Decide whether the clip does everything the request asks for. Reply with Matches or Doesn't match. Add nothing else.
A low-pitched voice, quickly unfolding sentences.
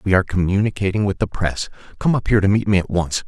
Matches